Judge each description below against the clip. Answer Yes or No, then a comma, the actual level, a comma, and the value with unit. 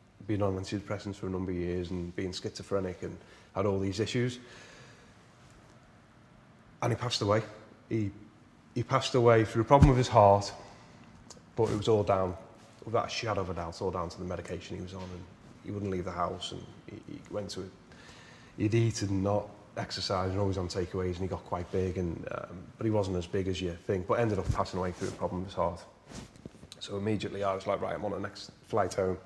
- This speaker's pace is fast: Yes, fast, 220 wpm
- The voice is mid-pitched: No, low, 100 Hz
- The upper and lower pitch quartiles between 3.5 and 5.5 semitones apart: No, average, 2.7 semitones